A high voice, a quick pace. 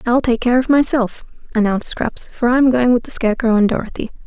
Yes: high, 240 Hz; fast, 210 wpm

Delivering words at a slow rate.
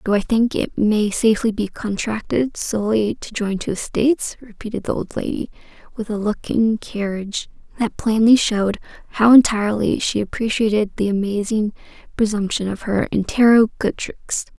No: average, 145 wpm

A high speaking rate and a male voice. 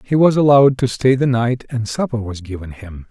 Yes: fast, 230 wpm; male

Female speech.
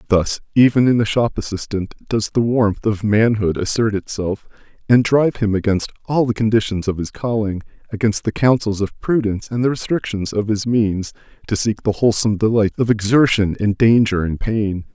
No: male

